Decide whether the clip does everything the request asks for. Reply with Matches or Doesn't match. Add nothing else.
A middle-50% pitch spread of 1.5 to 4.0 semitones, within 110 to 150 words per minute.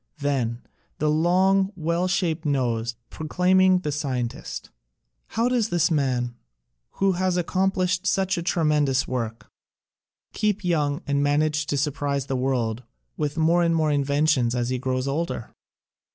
Doesn't match